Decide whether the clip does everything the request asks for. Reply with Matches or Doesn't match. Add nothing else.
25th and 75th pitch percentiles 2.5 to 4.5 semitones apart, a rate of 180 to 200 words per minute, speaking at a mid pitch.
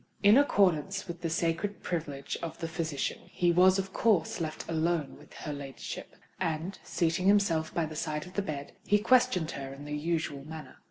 Matches